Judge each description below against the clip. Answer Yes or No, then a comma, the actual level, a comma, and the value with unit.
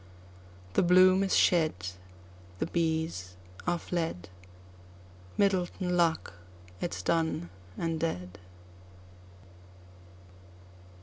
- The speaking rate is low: Yes, slow, 70 wpm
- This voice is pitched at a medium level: Yes, medium, 155 Hz